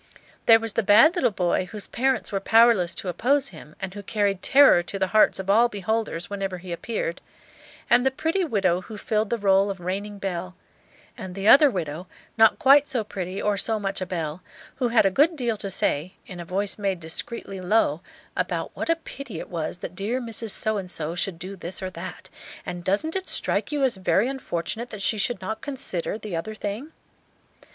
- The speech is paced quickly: Yes, fast, 210 wpm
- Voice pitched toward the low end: No, high, 200 Hz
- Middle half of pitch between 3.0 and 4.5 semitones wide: Yes, average, 4.1 semitones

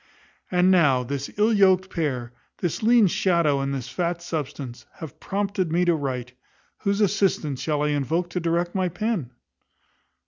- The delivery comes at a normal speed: Yes, average, 160 wpm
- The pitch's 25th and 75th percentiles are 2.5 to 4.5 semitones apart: No, average, 5.0 semitones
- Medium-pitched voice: Yes, medium, 170 Hz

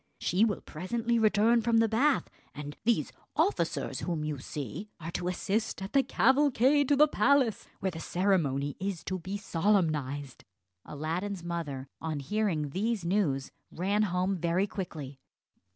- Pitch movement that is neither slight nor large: No, wide, 5.9 semitones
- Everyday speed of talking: Yes, average, 150 wpm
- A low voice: No, medium, 185 Hz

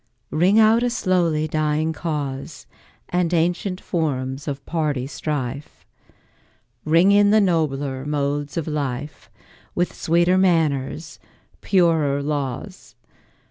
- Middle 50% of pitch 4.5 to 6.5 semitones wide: No, average, 3.8 semitones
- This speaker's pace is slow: Yes, slow, 105 wpm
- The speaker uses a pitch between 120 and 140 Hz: No, medium, 155 Hz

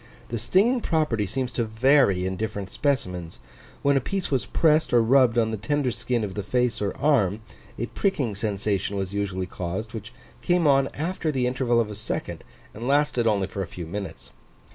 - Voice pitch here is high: No, low, 115 Hz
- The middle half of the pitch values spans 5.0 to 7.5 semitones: Yes, average, 5.3 semitones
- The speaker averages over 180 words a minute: Yes, average, 190 wpm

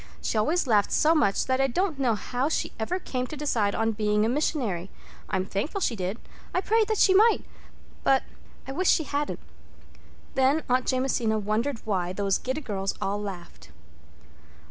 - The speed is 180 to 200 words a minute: No, average, 165 wpm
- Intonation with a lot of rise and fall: Yes, wide, 6.2 semitones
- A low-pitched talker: No, very high, 250 Hz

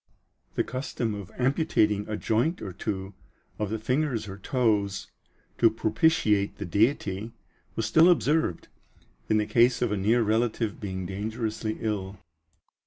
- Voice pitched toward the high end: No, low, 110 Hz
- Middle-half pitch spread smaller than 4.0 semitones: Yes, average, 3.1 semitones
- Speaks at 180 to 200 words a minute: No, average, 140 wpm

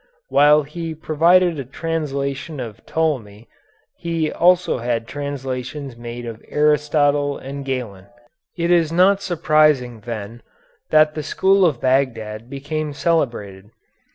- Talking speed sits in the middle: No, slow, 120 wpm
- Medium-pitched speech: Yes, medium, 145 Hz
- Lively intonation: No, average, 4.6 semitones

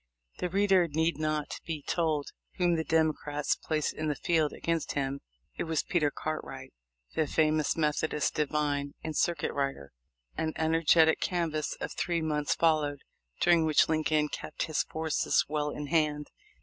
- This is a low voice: No, medium, 155 Hz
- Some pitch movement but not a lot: No, narrow, 1.5 semitones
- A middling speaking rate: Yes, average, 150 wpm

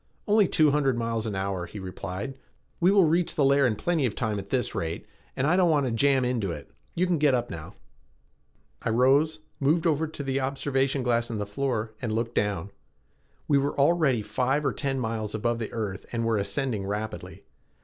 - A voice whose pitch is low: Yes, low, 125 Hz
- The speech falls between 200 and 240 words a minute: Yes, fast, 205 wpm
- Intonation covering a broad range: No, average, 4.7 semitones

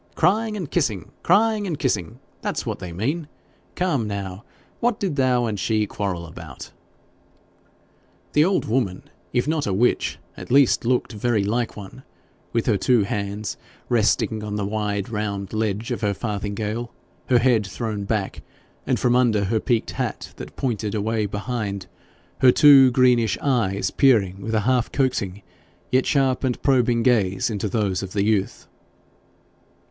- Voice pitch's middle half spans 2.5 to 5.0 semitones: Yes, average, 4.0 semitones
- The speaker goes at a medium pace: Yes, average, 155 wpm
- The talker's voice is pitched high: No, low, 110 Hz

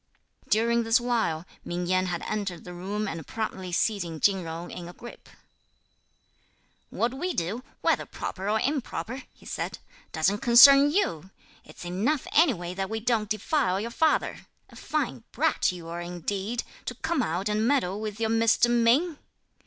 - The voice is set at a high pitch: Yes, high, 215 Hz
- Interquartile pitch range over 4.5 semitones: Yes, average, 5.1 semitones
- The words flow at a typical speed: Yes, average, 160 wpm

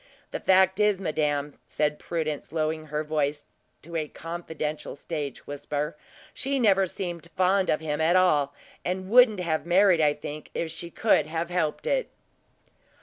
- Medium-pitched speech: Yes, medium, 165 Hz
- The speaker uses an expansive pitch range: No, average, 3.7 semitones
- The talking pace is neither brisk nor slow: Yes, average, 160 wpm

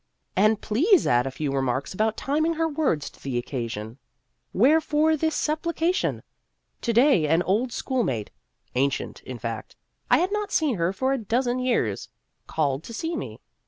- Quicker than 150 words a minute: Yes, average, 165 wpm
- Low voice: No, high, 225 Hz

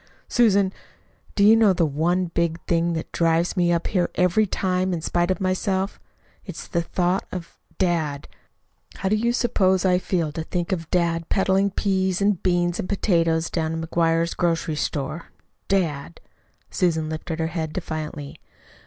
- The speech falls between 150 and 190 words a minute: Yes, average, 160 wpm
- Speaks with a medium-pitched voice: Yes, medium, 175 Hz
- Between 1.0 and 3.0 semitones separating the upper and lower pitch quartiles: Yes, narrow, 2.5 semitones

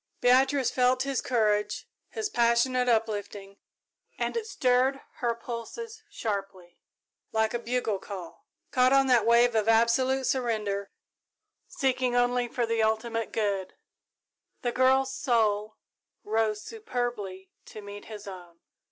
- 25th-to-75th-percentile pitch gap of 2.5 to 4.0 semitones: Yes, average, 3.3 semitones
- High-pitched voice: Yes, high, 235 Hz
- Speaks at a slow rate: Yes, slow, 125 wpm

